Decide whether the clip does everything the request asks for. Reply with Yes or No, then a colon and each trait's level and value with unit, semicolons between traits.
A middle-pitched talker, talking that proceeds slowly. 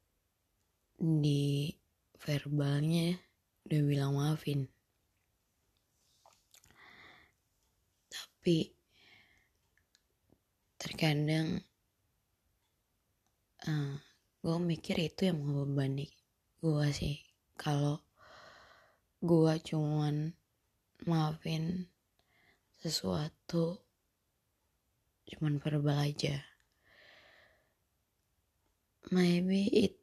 Yes: medium, 145 Hz; slow, 50 wpm